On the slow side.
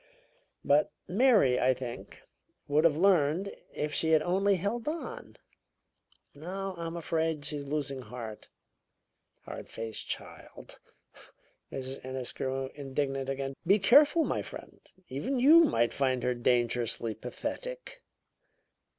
Yes: slow, 120 wpm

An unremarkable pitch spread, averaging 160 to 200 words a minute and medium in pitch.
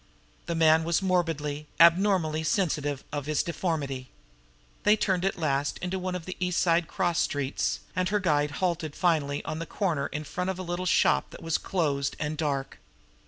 Yes: average, 3.6 semitones; average, 180 wpm; medium, 165 Hz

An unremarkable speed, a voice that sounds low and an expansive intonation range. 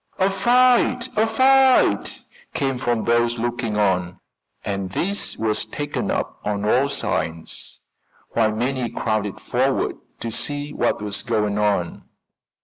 No: slow, 130 wpm; low, 120 Hz; wide, 6.0 semitones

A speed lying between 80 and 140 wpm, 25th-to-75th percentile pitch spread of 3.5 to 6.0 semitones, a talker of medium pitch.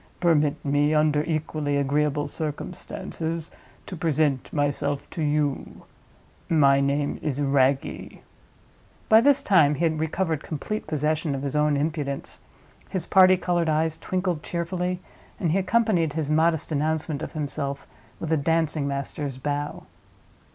No: slow, 135 wpm; narrow, 2.4 semitones; medium, 155 Hz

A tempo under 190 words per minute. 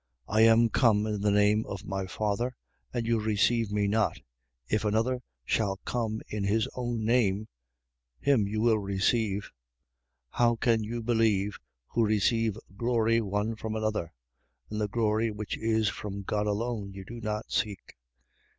Yes: average, 160 wpm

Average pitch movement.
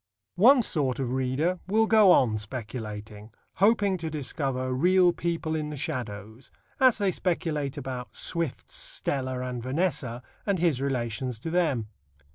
No: wide, 6.1 semitones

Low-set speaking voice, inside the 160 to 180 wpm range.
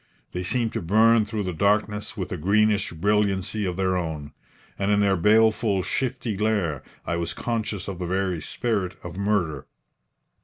Yes: low, 100 Hz; average, 165 wpm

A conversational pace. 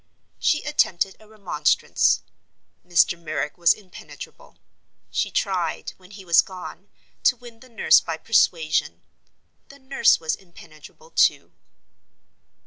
No: slow, 110 wpm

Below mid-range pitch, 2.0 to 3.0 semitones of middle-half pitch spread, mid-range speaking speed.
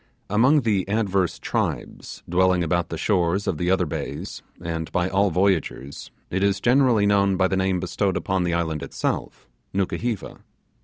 Yes: very low, 95 Hz; narrow, 2.5 semitones; average, 160 wpm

